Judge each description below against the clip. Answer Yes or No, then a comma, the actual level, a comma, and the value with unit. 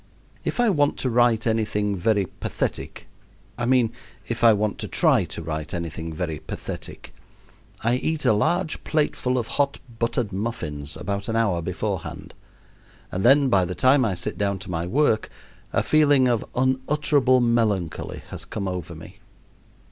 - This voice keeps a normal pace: Yes, average, 165 wpm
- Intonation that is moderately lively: No, wide, 5.7 semitones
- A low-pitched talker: Yes, low, 110 Hz